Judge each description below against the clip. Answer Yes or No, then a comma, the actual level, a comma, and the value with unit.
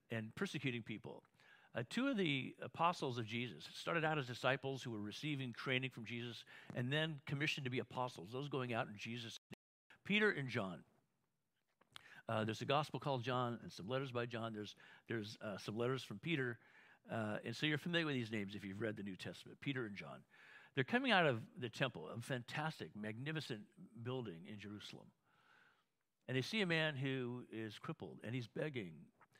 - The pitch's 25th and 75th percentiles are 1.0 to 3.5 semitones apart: No, average, 4.7 semitones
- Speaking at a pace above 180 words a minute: Yes, average, 190 wpm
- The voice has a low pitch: Yes, low, 125 Hz